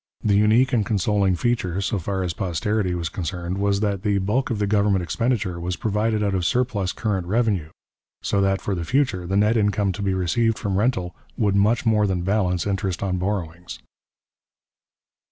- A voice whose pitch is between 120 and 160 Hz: No, low, 100 Hz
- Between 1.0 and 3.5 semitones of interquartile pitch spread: Yes, average, 2.8 semitones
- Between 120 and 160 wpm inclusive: No, average, 185 wpm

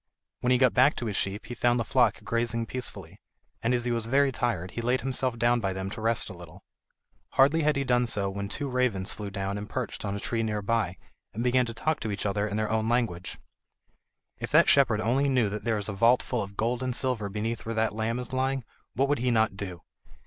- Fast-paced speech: Yes, fast, 245 wpm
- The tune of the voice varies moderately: Yes, average, 3.3 semitones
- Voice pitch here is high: No, low, 115 Hz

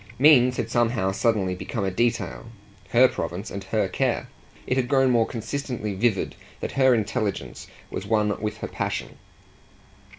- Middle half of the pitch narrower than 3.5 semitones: No, average, 3.9 semitones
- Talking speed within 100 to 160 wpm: Yes, average, 155 wpm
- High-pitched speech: No, low, 115 Hz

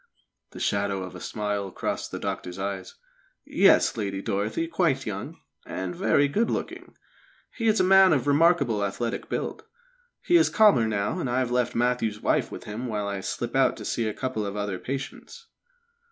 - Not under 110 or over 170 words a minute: No, average, 180 wpm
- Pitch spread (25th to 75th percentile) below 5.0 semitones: No, wide, 5.5 semitones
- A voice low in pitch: Yes, low, 115 Hz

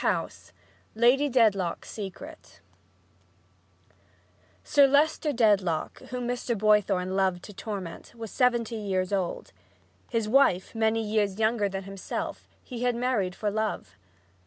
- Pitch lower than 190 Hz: No, high, 215 Hz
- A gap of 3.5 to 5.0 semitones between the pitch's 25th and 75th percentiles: Yes, average, 3.9 semitones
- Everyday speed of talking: No, slow, 125 wpm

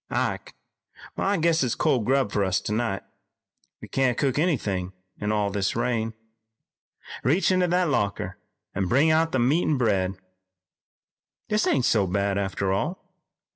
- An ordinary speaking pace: Yes, average, 150 wpm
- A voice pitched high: No, low, 120 Hz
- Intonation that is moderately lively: No, wide, 7.5 semitones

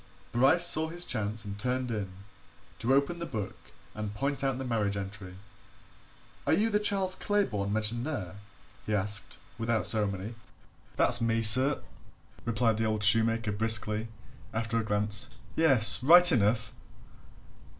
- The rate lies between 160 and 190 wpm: No, average, 140 wpm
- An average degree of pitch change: Yes, average, 4.2 semitones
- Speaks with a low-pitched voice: Yes, low, 115 Hz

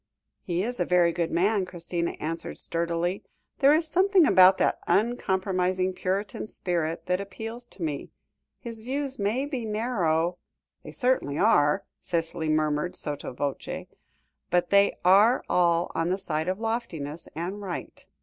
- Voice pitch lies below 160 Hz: No, medium, 185 Hz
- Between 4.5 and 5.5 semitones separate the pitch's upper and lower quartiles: Yes, average, 4.8 semitones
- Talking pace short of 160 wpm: Yes, average, 150 wpm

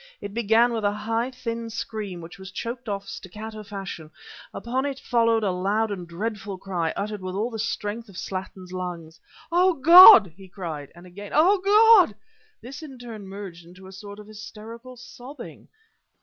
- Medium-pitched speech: No, high, 210 Hz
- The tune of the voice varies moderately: Yes, average, 3.7 semitones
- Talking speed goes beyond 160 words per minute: Yes, average, 175 wpm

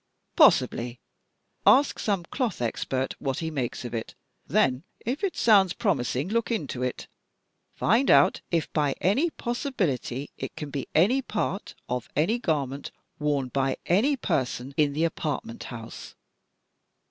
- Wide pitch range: Yes, wide, 8.6 semitones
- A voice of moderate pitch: Yes, medium, 155 Hz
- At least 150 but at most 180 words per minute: No, average, 140 wpm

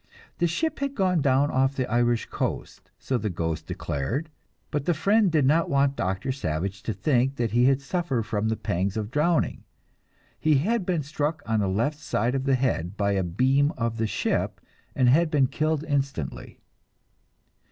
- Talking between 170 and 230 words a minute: Yes, average, 185 wpm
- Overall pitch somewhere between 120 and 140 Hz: Yes, low, 135 Hz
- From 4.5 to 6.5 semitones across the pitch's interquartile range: Yes, wide, 5.6 semitones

